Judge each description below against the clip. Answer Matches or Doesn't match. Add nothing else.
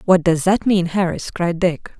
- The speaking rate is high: Matches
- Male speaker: Doesn't match